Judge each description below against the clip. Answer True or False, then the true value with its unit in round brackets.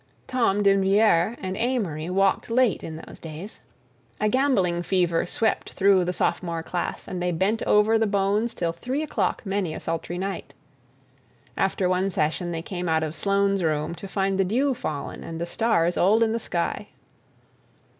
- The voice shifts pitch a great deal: False (3.7 semitones)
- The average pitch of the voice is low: False (190 Hz)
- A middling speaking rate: True (170 wpm)